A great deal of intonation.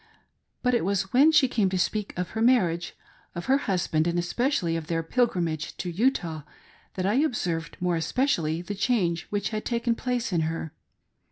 Yes: wide, 6.2 semitones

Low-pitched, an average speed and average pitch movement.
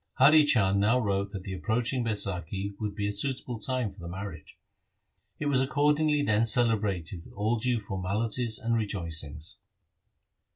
Yes: low, 105 Hz; average, 155 wpm; average, 4.1 semitones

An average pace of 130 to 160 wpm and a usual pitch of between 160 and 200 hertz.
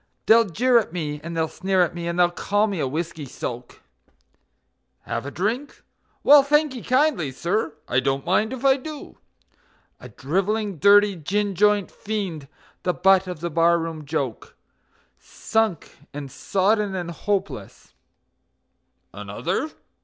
Yes: average, 145 wpm; medium, 185 Hz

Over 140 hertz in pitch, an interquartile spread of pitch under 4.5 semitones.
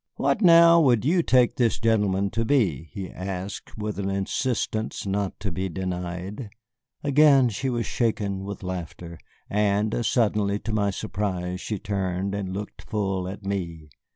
No: low, 100 Hz; average, 3.4 semitones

